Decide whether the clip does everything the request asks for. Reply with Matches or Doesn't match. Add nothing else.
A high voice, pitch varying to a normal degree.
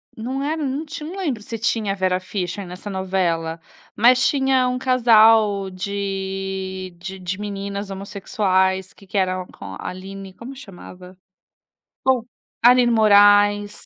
Matches